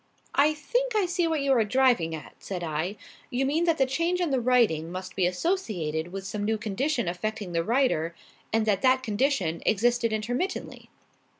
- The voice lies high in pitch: Yes, high, 230 Hz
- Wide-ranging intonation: Yes, wide, 7.0 semitones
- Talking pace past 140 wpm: Yes, average, 185 wpm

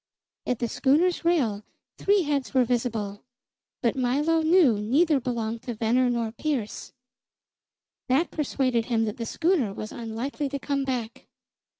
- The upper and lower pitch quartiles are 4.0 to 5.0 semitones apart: Yes, average, 4.3 semitones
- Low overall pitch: No, very high, 250 Hz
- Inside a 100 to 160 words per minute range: Yes, average, 140 wpm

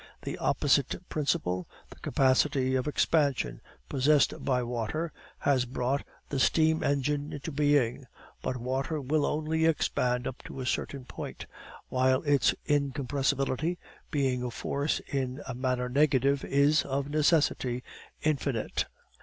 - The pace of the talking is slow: Yes, slow, 130 wpm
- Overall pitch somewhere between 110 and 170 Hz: Yes, low, 135 Hz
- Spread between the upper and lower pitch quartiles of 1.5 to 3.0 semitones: Yes, narrow, 2.5 semitones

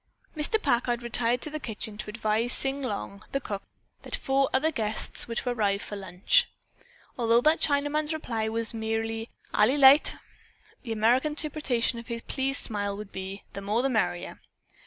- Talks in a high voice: Yes, high, 235 Hz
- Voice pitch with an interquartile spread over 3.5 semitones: Yes, average, 4.1 semitones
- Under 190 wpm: Yes, average, 170 wpm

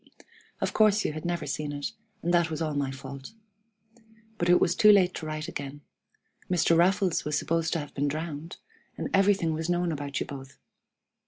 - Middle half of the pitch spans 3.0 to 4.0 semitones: Yes, average, 3.3 semitones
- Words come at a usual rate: Yes, average, 190 wpm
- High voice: No, medium, 160 Hz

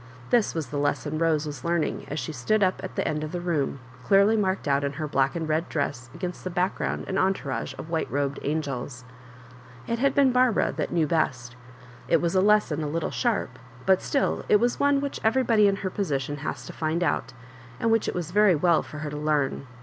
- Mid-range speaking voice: Yes, medium, 165 Hz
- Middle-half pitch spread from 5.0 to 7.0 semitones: Yes, wide, 5.4 semitones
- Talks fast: Yes, fast, 225 wpm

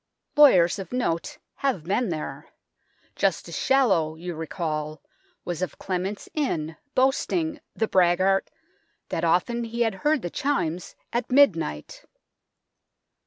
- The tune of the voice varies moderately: No, wide, 7.3 semitones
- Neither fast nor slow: No, slow, 120 wpm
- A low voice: No, high, 190 Hz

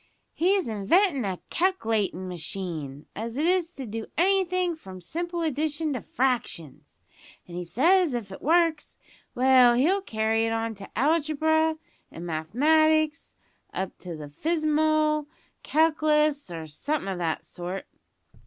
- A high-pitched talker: Yes, very high, 275 Hz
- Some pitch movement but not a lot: No, wide, 8.5 semitones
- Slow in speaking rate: Yes, slow, 130 wpm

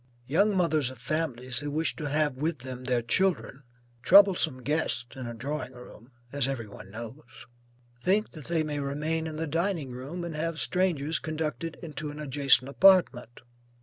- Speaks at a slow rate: No, average, 170 wpm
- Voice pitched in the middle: Yes, medium, 150 Hz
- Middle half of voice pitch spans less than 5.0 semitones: Yes, average, 4.2 semitones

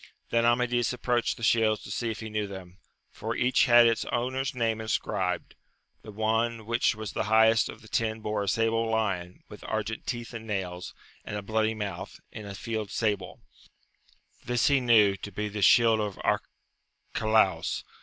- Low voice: Yes, low, 110 Hz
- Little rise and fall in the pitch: Yes, narrow, 2.0 semitones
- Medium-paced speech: Yes, average, 175 wpm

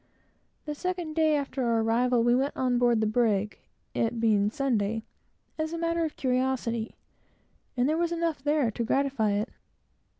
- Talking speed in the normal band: Yes, average, 165 wpm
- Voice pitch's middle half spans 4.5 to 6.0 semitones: Yes, average, 4.9 semitones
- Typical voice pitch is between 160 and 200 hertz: No, very high, 250 Hz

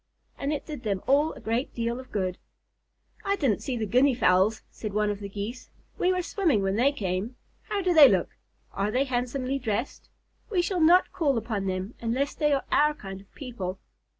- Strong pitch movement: Yes, wide, 5.8 semitones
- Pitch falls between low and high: No, high, 245 Hz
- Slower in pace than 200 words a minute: No, fast, 205 wpm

